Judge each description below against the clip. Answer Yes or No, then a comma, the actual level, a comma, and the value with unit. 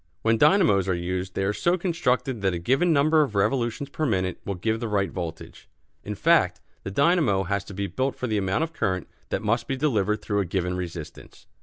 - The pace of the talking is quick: Yes, fast, 215 wpm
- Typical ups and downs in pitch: No, wide, 6.3 semitones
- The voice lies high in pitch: No, low, 105 Hz